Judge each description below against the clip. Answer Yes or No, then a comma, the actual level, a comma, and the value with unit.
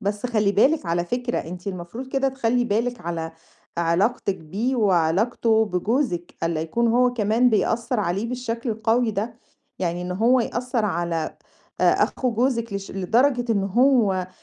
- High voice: Yes, high, 220 Hz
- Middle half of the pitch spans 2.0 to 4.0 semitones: No, average, 5.1 semitones